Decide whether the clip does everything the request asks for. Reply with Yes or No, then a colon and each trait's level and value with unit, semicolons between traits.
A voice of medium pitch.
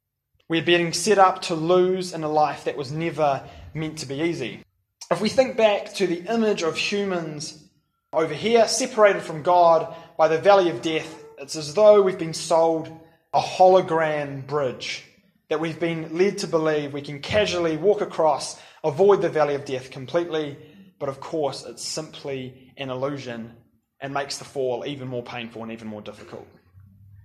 Yes: medium, 160 Hz